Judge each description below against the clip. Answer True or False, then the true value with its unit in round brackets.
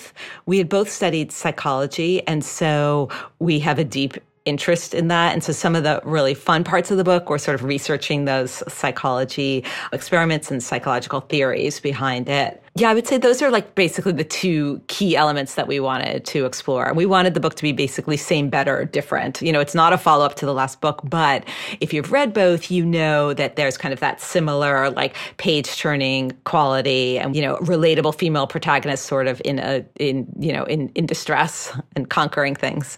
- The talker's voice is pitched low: False (150 Hz)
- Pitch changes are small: False (3.7 semitones)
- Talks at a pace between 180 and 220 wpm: True (200 wpm)